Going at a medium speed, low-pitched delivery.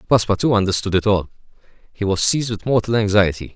Yes: average, 170 wpm; low, 105 Hz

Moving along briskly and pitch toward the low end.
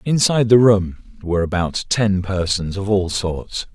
No: average, 160 wpm; low, 100 Hz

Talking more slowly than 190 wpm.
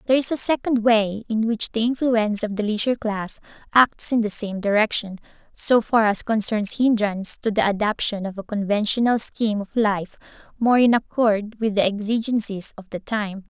Yes: average, 180 wpm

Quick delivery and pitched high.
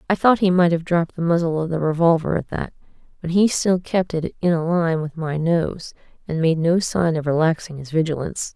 No: fast, 225 wpm; medium, 165 Hz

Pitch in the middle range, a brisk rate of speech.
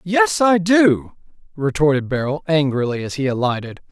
No: medium, 150 Hz; average, 140 wpm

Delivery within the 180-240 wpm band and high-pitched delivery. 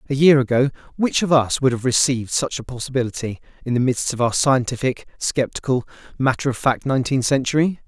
No: average, 185 wpm; low, 130 Hz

